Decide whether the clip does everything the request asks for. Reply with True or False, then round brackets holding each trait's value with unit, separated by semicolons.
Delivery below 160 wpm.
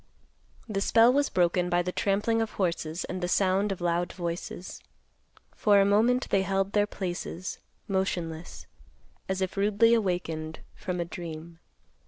True (150 wpm)